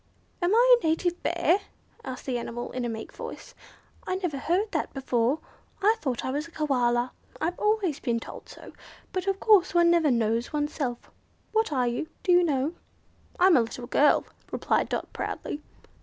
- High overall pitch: Yes, very high, 305 Hz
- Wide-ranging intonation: Yes, wide, 6.2 semitones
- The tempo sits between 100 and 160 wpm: No, average, 180 wpm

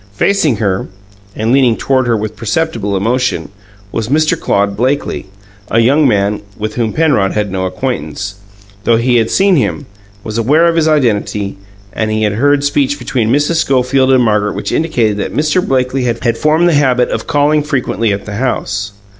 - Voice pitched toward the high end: No, low, 120 Hz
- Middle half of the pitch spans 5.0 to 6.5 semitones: Yes, wide, 5.5 semitones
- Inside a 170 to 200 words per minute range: Yes, average, 175 wpm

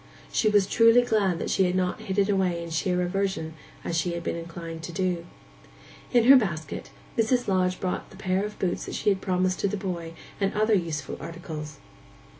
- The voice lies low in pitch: No, medium, 185 Hz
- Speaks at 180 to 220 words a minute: Yes, average, 200 wpm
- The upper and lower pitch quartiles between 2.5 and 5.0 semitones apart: Yes, average, 3.1 semitones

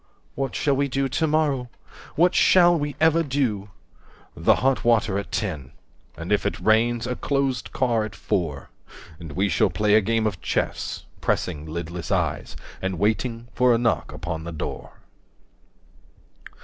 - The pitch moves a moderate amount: No, wide, 6.1 semitones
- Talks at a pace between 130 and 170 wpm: Yes, average, 160 wpm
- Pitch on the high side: No, low, 115 Hz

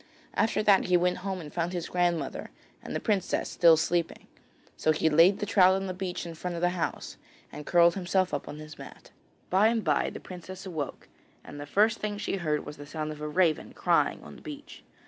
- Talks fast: Yes, fast, 225 wpm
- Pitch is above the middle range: No, medium, 175 Hz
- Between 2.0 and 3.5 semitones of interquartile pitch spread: Yes, average, 3.1 semitones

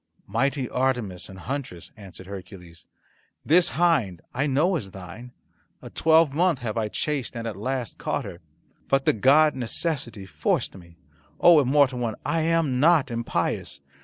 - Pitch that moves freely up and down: Yes, wide, 6.9 semitones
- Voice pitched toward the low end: Yes, low, 125 Hz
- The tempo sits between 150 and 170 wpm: Yes, average, 155 wpm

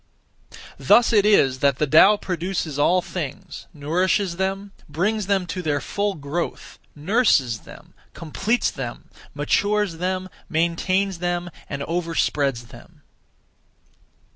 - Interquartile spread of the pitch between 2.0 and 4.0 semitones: No, average, 4.6 semitones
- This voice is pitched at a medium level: Yes, medium, 175 Hz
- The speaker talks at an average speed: No, slow, 115 wpm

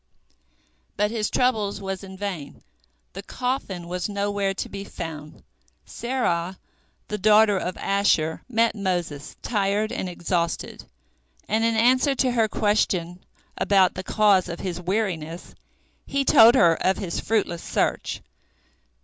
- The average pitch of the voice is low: No, high, 195 Hz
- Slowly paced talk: Yes, slow, 130 wpm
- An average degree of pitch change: Yes, average, 3.6 semitones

